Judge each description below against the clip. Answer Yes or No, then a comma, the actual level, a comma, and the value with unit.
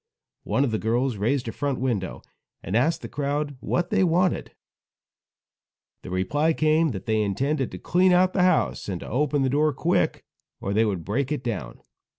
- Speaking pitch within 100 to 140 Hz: Yes, low, 135 Hz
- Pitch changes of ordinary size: No, wide, 5.7 semitones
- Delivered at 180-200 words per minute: Yes, average, 185 wpm